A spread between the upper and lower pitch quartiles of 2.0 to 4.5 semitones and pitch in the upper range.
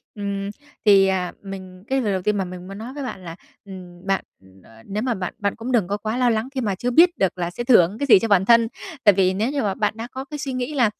Yes: average, 4.2 semitones; high, 205 Hz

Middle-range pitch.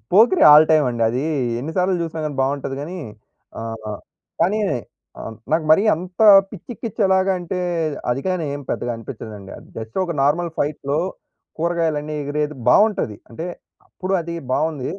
Yes: medium, 155 Hz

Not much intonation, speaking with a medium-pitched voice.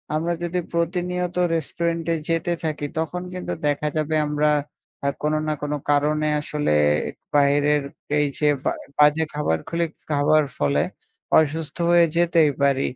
Yes: narrow, 2.3 semitones; medium, 155 Hz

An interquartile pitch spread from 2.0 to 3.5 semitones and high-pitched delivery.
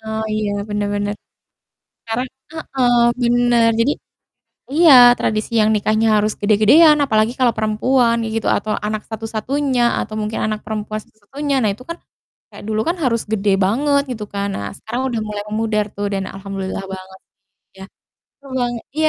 Yes: average, 2.8 semitones; high, 220 Hz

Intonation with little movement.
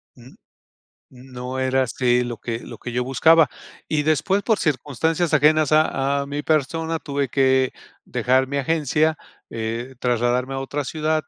No: average, 3.7 semitones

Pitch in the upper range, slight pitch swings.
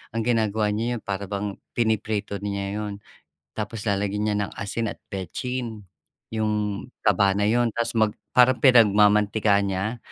No: low, 105 Hz; narrow, 1.9 semitones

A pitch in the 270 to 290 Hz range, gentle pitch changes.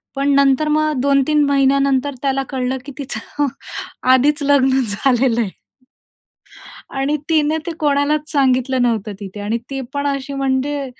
Yes: very high, 275 Hz; narrow, 1.8 semitones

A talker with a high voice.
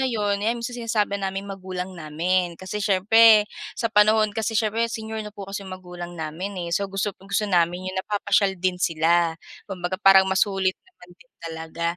Yes: high, 195 Hz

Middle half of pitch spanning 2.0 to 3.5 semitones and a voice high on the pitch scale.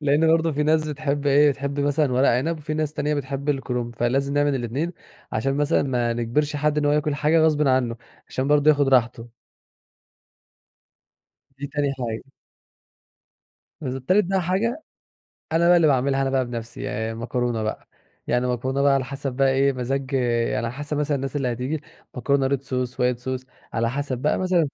No: average, 2.9 semitones; medium, 140 Hz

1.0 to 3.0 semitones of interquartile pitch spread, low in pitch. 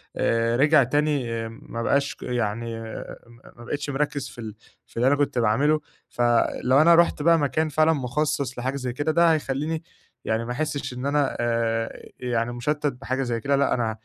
No: average, 3.8 semitones; low, 130 Hz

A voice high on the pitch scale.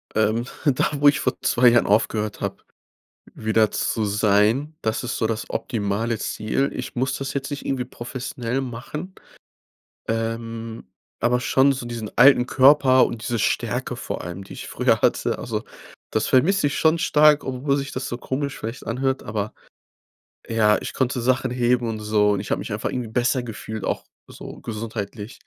No: low, 120 Hz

